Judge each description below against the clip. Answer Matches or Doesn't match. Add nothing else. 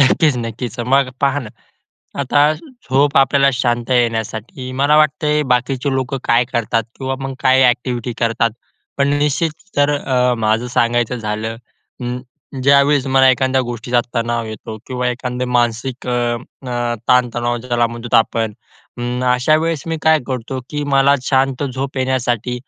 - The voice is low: Matches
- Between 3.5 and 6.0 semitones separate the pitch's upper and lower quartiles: Doesn't match